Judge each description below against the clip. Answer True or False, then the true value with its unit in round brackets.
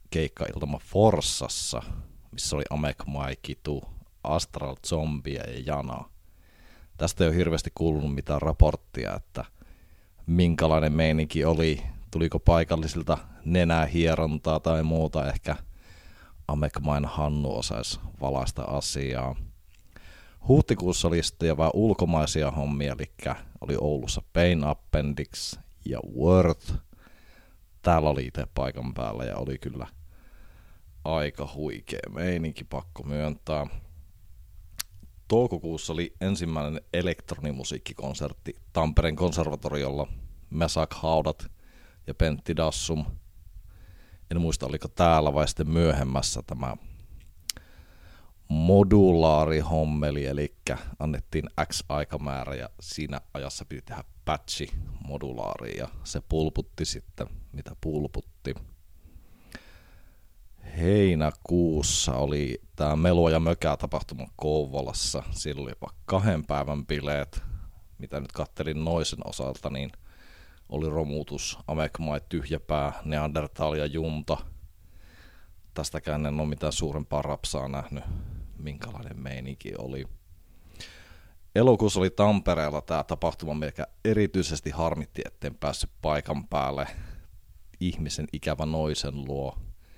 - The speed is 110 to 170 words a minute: False (100 wpm)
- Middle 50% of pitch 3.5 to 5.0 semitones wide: False (2.5 semitones)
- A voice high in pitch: False (80 Hz)